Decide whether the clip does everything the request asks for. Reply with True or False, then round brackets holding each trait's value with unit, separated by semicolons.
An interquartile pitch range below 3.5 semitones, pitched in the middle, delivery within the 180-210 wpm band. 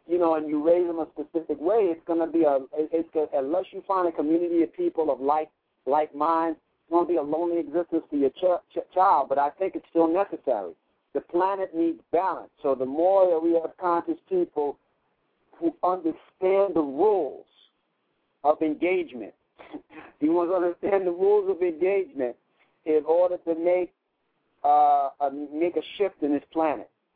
True (3.1 semitones; 165 Hz; 185 wpm)